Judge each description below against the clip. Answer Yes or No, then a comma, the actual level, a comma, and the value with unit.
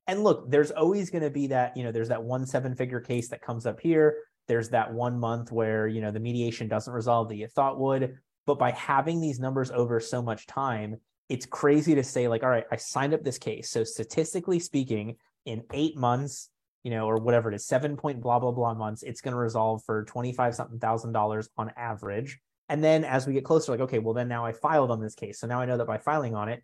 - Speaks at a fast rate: Yes, fast, 245 wpm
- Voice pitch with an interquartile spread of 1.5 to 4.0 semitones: Yes, average, 3.4 semitones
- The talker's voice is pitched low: Yes, low, 120 Hz